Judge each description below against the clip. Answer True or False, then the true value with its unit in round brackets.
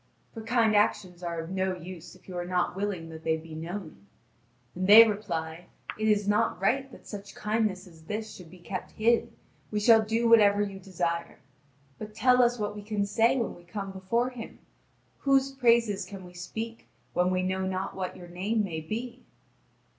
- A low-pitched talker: False (200 Hz)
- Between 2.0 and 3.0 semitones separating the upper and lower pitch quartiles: False (3.8 semitones)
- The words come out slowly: False (190 wpm)